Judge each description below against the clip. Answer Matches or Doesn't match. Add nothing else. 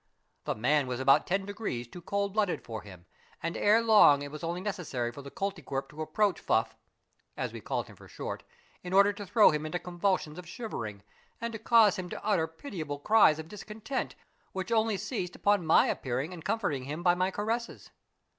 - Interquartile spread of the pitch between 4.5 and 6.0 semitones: Matches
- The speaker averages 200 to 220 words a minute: Matches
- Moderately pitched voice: Matches